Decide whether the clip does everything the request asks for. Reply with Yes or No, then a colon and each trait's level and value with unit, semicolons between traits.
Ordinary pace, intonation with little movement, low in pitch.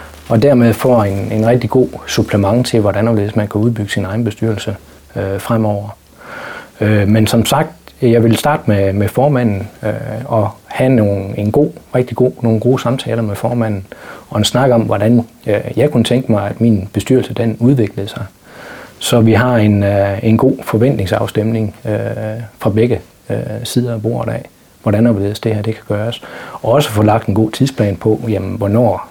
Yes: average, 185 wpm; narrow, 2.3 semitones; low, 110 Hz